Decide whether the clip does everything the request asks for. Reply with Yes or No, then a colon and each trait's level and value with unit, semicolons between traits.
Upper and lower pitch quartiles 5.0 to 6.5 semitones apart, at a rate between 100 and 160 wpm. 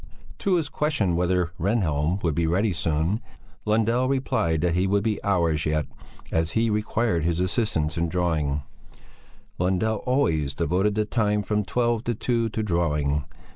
Yes: average, 5.3 semitones; average, 155 wpm